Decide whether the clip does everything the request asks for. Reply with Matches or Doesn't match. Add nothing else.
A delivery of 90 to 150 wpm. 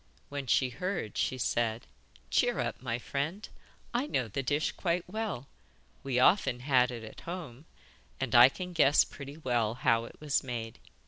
Doesn't match